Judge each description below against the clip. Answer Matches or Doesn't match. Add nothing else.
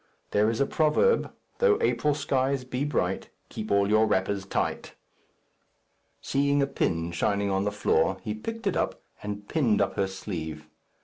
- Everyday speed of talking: Matches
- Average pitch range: Doesn't match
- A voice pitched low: Matches